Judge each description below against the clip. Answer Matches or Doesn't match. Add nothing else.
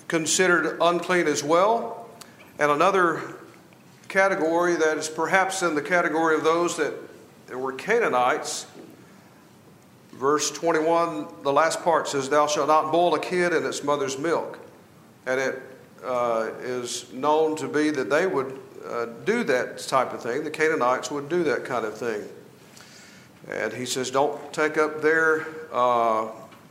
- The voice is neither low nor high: Matches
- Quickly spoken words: Doesn't match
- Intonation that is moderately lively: Matches